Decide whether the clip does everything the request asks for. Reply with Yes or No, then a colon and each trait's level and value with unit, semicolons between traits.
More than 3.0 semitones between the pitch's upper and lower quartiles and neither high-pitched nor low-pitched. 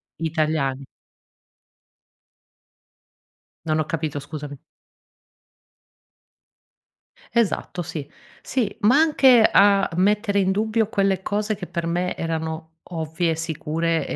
Yes: average, 4.3 semitones; medium, 170 Hz